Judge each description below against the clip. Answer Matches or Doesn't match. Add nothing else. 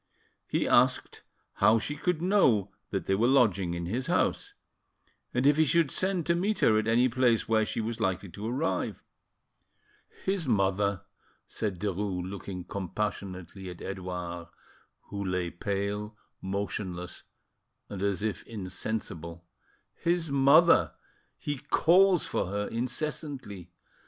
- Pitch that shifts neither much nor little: Doesn't match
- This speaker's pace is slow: Matches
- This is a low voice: Matches